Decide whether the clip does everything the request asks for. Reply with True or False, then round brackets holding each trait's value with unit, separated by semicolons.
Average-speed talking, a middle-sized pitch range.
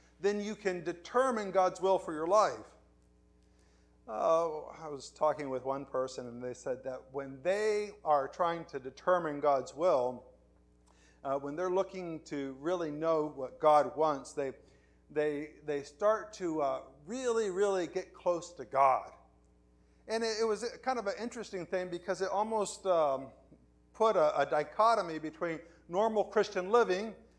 False (155 wpm; 6.3 semitones)